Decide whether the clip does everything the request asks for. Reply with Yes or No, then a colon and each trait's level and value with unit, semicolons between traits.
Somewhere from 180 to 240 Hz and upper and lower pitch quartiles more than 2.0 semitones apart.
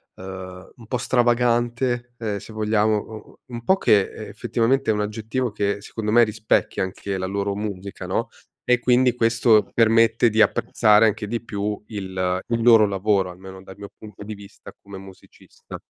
No: low, 105 Hz; average, 2.7 semitones